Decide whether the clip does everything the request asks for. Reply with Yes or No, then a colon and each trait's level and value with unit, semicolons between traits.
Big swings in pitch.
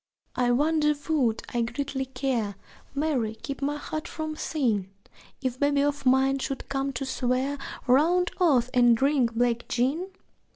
No: average, 3.1 semitones